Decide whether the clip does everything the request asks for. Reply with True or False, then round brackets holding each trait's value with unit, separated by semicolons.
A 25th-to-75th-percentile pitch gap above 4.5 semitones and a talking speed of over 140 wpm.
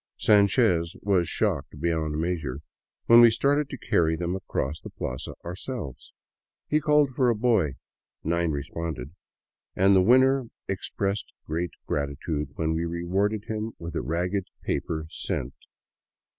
False (5.5 semitones; 135 wpm)